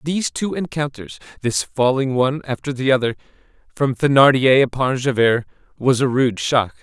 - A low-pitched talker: Yes, low, 130 Hz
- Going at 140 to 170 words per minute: Yes, average, 150 wpm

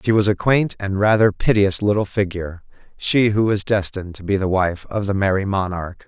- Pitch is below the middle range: Yes, low, 100 Hz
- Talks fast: Yes, fast, 210 wpm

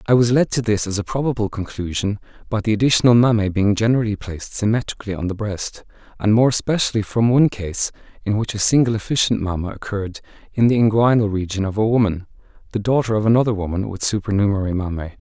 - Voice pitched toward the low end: Yes, low, 105 Hz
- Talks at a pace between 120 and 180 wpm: No, average, 190 wpm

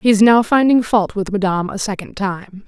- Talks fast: Yes, fast, 225 wpm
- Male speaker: No, female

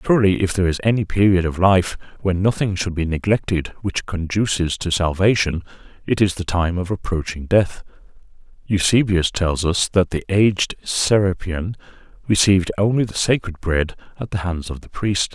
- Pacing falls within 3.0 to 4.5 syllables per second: No, 5.1 syllables/s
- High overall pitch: No, very low, 95 Hz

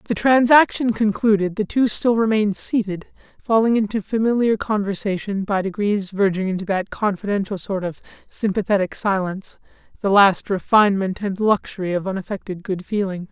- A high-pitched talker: Yes, high, 205 Hz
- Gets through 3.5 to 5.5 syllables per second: Yes, 5.3 syllables/s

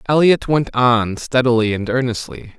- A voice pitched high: No, low, 125 Hz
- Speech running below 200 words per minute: Yes, average, 140 wpm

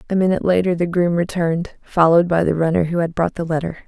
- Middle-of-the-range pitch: Yes, medium, 170 Hz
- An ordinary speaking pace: No, fast, 230 wpm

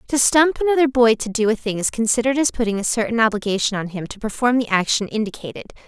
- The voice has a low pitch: No, high, 230 Hz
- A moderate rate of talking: No, fast, 225 wpm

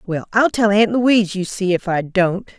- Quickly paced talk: Yes, fast, 230 wpm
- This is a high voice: Yes, high, 195 Hz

